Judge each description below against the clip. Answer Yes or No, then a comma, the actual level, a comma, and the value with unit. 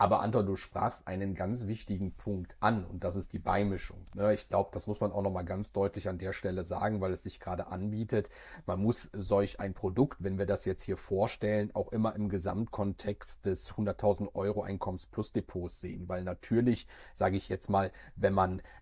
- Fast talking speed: Yes, fast, 200 wpm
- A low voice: Yes, low, 100 Hz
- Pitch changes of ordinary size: No, narrow, 1.9 semitones